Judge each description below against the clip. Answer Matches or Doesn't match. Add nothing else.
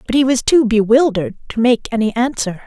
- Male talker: Doesn't match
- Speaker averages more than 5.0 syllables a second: Matches